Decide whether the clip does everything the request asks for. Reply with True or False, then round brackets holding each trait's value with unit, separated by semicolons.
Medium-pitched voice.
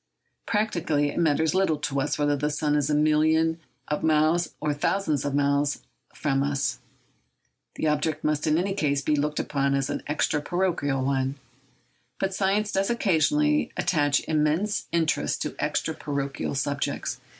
True (150 Hz)